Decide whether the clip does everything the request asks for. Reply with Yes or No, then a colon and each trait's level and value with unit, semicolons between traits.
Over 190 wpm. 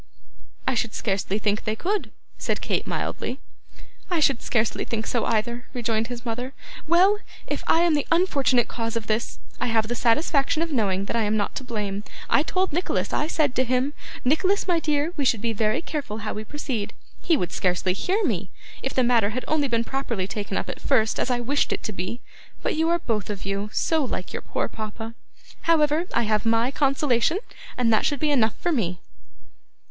Yes: fast, 205 wpm